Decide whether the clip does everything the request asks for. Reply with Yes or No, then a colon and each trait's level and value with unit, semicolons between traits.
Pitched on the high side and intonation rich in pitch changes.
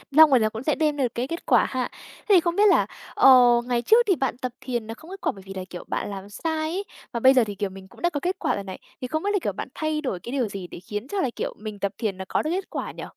Yes: very high, 250 Hz; wide, 7.3 semitones